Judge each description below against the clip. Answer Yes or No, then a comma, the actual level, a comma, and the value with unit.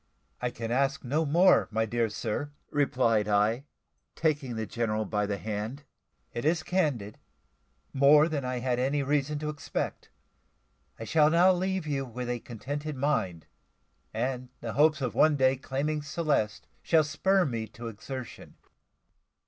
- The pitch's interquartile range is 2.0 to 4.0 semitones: No, average, 4.6 semitones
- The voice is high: No, low, 135 Hz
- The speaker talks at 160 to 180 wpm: No, average, 150 wpm